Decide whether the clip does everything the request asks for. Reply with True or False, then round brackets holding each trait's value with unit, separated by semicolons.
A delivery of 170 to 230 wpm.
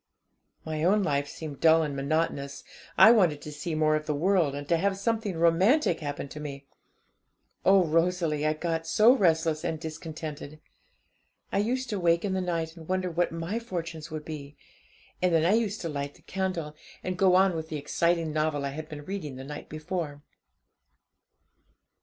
True (185 wpm)